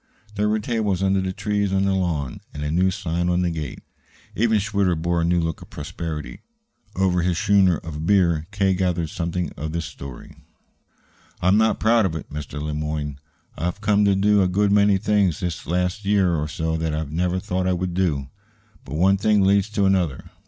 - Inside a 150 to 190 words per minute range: No, average, 200 wpm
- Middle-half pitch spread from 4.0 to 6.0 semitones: No, average, 3.5 semitones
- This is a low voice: Yes, very low, 90 Hz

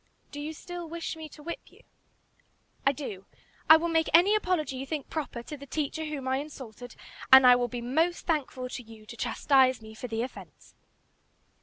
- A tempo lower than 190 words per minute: No, average, 195 wpm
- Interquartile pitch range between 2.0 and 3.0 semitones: No, average, 4.3 semitones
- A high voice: Yes, very high, 280 Hz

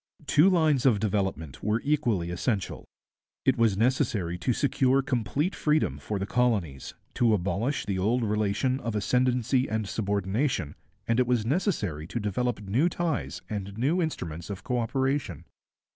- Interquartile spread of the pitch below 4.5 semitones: No, average, 5.1 semitones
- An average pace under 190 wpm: Yes, average, 150 wpm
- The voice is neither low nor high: No, low, 115 Hz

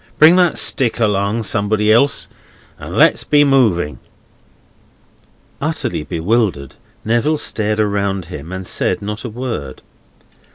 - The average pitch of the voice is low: Yes, low, 110 Hz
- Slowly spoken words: Yes, slow, 120 wpm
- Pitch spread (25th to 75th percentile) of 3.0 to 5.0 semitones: Yes, average, 4.3 semitones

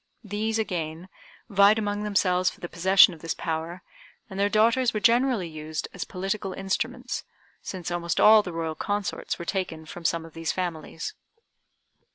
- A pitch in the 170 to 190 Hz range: Yes, medium, 185 Hz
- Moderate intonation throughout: Yes, average, 3.9 semitones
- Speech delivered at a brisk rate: No, average, 165 wpm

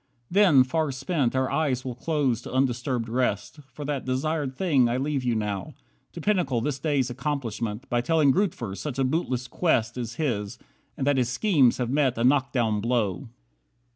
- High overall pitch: No, low, 130 Hz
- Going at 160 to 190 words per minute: Yes, average, 180 wpm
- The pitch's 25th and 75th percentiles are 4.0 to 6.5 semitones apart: No, average, 3.6 semitones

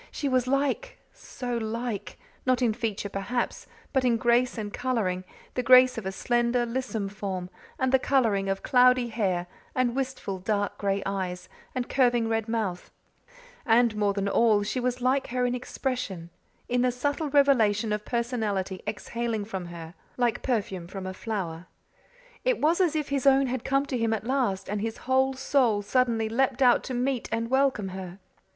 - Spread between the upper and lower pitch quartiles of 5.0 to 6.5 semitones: No, average, 3.9 semitones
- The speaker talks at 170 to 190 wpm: Yes, average, 175 wpm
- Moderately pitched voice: No, high, 235 Hz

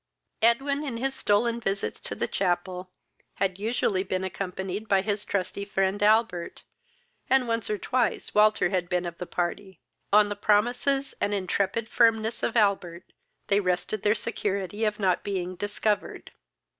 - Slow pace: No, average, 155 wpm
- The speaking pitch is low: No, high, 205 Hz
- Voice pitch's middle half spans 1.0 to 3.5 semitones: Yes, average, 2.9 semitones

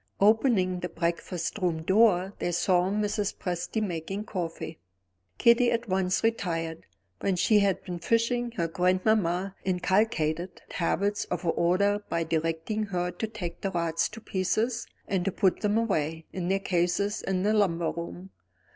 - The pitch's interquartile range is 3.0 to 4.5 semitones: Yes, average, 3.4 semitones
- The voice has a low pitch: No, medium, 185 Hz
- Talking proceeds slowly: No, average, 150 wpm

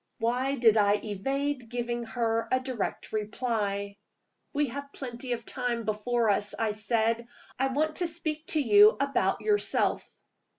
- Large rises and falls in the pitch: No, average, 3.7 semitones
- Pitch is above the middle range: Yes, high, 235 Hz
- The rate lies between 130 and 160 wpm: Yes, average, 145 wpm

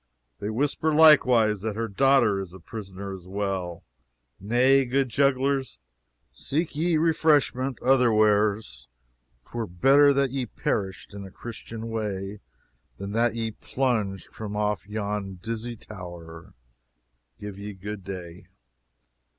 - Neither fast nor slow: No, slow, 125 wpm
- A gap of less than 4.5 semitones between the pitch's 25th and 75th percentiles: No, average, 4.9 semitones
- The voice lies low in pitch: Yes, low, 110 Hz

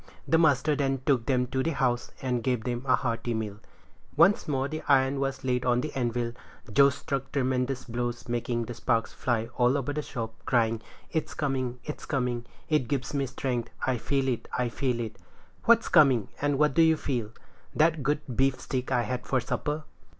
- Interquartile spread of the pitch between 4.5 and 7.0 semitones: No, average, 2.7 semitones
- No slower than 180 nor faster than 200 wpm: Yes, average, 190 wpm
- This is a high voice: No, low, 130 Hz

